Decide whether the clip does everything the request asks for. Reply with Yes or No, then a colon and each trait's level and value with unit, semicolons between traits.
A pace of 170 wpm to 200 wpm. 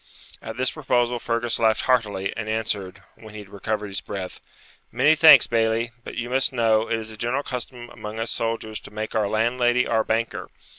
Yes: average, 195 wpm